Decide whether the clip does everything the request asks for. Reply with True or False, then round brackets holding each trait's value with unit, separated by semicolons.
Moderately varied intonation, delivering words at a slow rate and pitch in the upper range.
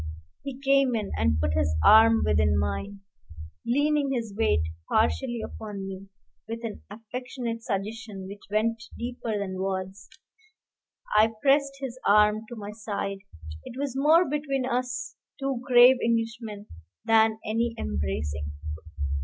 True (4.1 semitones; 130 wpm; 225 Hz)